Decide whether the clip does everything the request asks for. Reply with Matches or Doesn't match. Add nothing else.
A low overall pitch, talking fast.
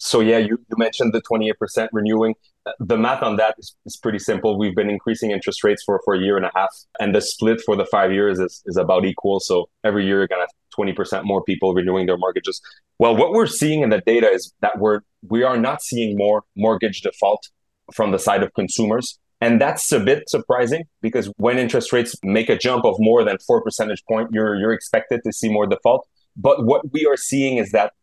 Matches